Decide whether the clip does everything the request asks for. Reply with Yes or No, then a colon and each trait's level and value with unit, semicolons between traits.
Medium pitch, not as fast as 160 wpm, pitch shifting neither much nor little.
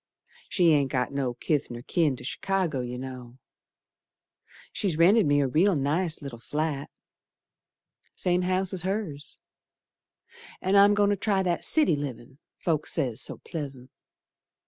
No: medium, 155 Hz; average, 145 wpm; wide, 5.8 semitones